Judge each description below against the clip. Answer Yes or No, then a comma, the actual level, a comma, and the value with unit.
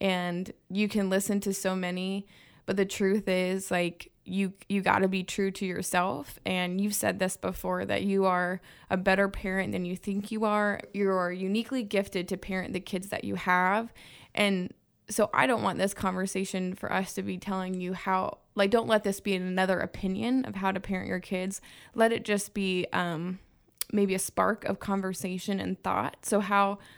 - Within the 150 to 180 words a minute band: No, average, 190 wpm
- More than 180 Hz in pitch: Yes, high, 190 Hz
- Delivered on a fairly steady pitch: Yes, narrow, 1.4 semitones